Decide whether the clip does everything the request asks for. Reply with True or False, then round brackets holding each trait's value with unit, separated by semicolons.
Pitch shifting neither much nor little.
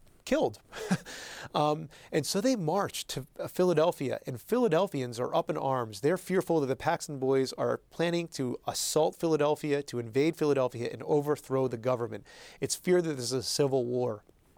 True (3.9 semitones)